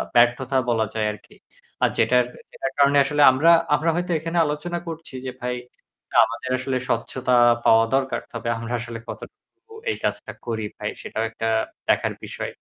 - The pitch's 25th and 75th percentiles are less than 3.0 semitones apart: No, average, 4.0 semitones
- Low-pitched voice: Yes, low, 130 Hz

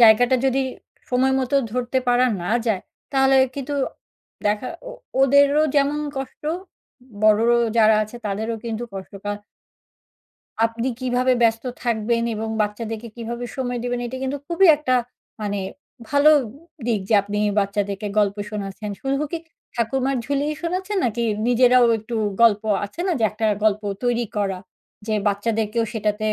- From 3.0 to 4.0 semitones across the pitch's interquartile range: Yes, average, 3.7 semitones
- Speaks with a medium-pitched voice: No, high, 235 Hz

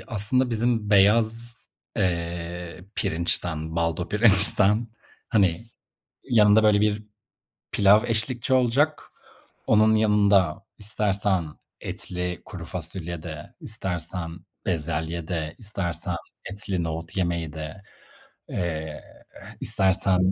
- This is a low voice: Yes, very low, 95 Hz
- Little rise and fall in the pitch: No, average, 4.0 semitones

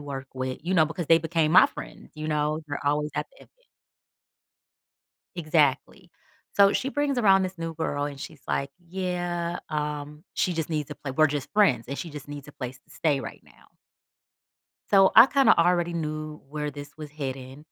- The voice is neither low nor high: Yes, medium, 155 Hz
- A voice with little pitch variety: No, average, 3.1 semitones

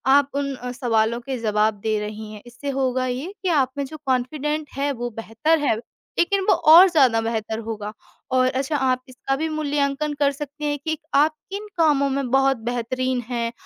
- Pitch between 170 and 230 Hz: No, very high, 265 Hz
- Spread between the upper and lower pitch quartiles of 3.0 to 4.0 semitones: Yes, average, 3.4 semitones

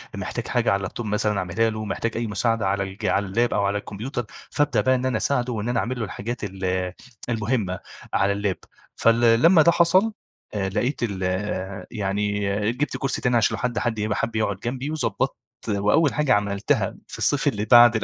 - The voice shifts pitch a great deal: No, average, 3.3 semitones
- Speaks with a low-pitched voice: Yes, low, 110 Hz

